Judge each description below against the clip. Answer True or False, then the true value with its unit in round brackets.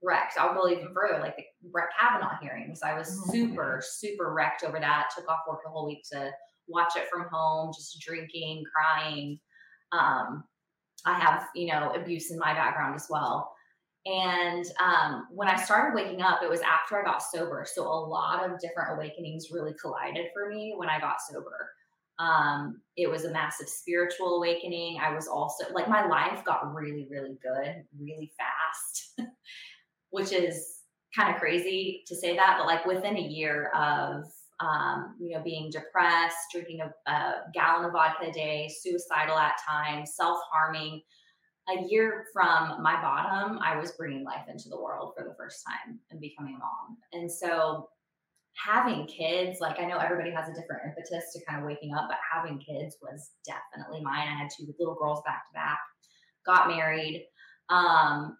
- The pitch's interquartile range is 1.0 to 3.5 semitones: True (2.5 semitones)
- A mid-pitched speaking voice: True (165 Hz)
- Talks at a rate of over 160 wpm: True (180 wpm)